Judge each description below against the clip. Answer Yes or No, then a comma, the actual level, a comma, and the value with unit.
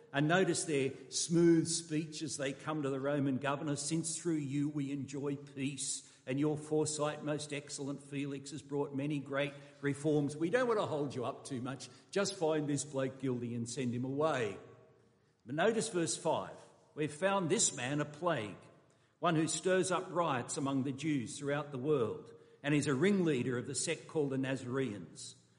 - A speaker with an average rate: Yes, average, 185 wpm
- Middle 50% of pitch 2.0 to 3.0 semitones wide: Yes, narrow, 2.6 semitones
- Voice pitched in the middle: Yes, medium, 145 Hz